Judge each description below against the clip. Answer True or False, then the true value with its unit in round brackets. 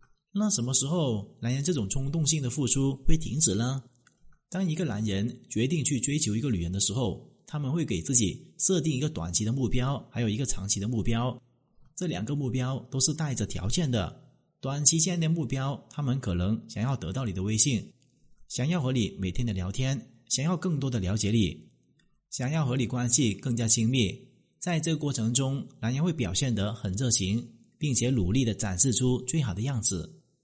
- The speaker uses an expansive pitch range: False (4.5 semitones)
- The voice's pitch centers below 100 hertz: False (125 Hz)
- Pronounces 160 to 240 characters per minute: False (285 characters per minute)